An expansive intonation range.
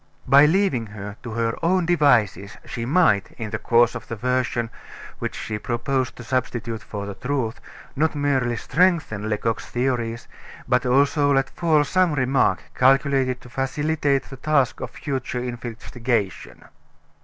No: average, 3.6 semitones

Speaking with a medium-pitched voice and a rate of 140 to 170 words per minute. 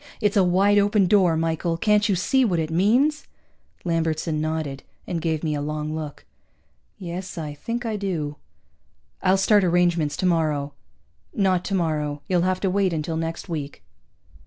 Yes: medium, 170 Hz; average, 160 wpm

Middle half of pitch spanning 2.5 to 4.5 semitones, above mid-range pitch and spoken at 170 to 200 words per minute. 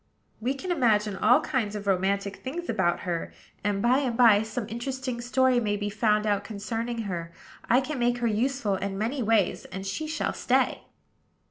Yes: average, 3.9 semitones; high, 225 Hz; average, 180 wpm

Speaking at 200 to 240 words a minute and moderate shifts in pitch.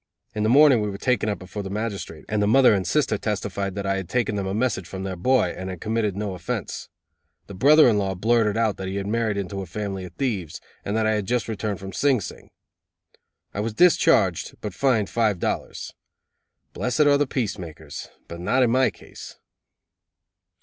Yes: fast, 205 wpm; average, 3.4 semitones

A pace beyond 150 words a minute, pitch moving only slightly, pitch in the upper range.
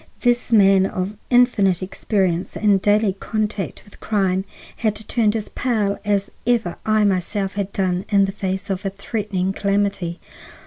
No: average, 145 wpm; narrow, 2.0 semitones; high, 200 Hz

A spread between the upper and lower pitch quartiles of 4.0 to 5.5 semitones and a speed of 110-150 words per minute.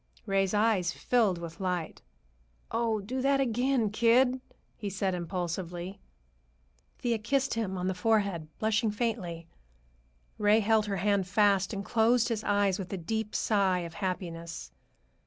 No: average, 3.5 semitones; average, 140 wpm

